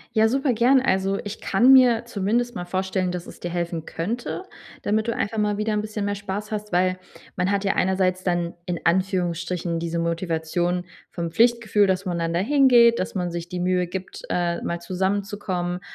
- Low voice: No, high, 190 Hz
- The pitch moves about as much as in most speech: Yes, average, 3.3 semitones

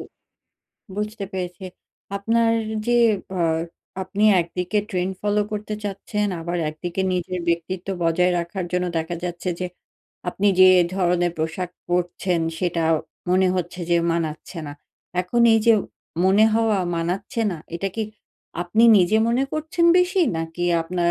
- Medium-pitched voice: Yes, medium, 180 Hz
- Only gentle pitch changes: No, average, 3.2 semitones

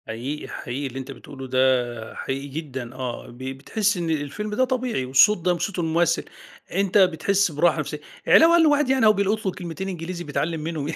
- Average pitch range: No, wide, 6.8 semitones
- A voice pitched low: No, medium, 165 Hz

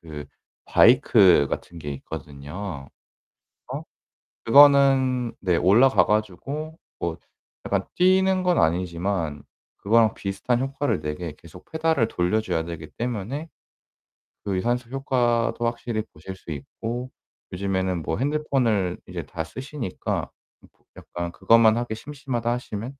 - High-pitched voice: No, low, 110 Hz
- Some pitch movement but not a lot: No, wide, 6.8 semitones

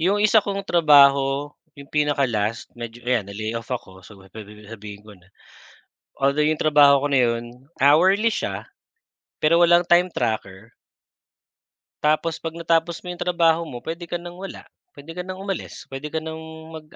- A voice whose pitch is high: No, medium, 150 Hz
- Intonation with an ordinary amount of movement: No, wide, 6.2 semitones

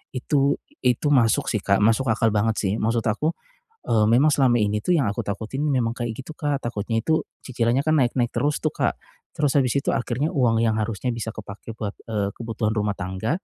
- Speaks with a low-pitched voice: Yes, low, 115 Hz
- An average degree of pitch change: Yes, average, 3.6 semitones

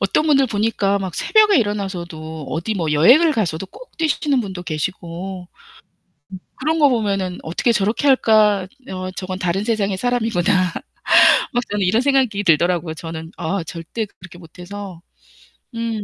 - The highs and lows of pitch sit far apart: No, average, 4.6 semitones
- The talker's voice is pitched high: Yes, high, 195 Hz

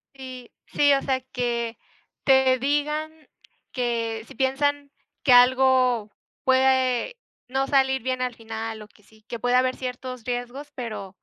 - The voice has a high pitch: Yes, very high, 255 Hz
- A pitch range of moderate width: No, narrow, 2.0 semitones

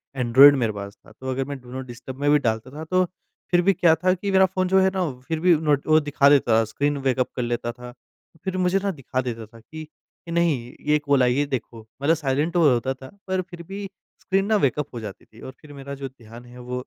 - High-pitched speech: No, medium, 140 Hz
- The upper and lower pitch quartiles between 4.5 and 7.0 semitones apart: Yes, wide, 5.4 semitones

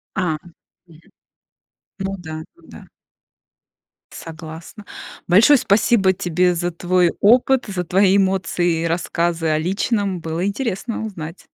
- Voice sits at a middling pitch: Yes, medium, 180 Hz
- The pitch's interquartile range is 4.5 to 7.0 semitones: No, average, 3.2 semitones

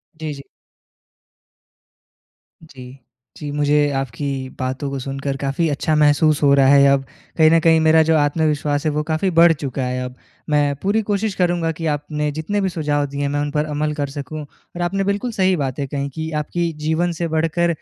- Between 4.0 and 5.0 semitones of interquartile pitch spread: No, narrow, 2.5 semitones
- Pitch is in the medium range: Yes, medium, 150 Hz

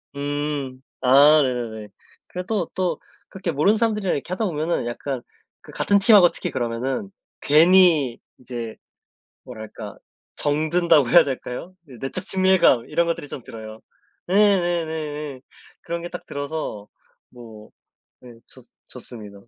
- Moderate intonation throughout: No, wide, 5.9 semitones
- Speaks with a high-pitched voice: No, medium, 145 Hz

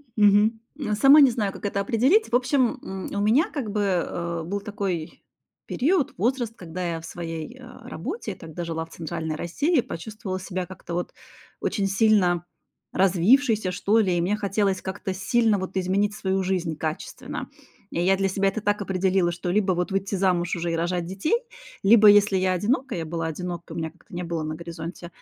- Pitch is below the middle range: No, high, 190 Hz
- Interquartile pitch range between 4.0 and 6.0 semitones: No, average, 3.5 semitones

